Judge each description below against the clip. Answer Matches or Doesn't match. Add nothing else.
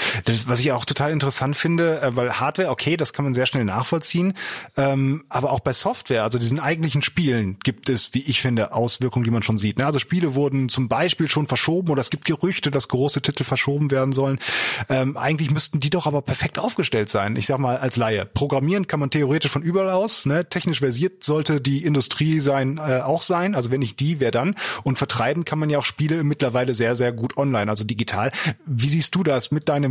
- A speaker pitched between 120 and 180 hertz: Matches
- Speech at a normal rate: Doesn't match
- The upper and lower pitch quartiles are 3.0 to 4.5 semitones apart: Matches